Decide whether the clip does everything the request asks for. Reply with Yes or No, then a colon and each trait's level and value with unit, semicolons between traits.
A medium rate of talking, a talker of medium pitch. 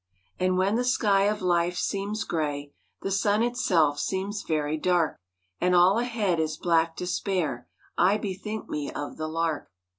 Yes: average, 155 wpm; medium, 180 Hz